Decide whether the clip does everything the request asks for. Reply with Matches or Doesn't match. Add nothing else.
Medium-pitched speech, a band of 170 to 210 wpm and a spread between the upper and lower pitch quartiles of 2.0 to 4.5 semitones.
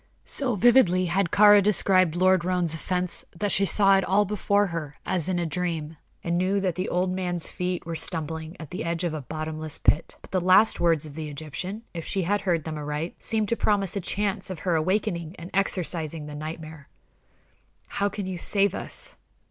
Matches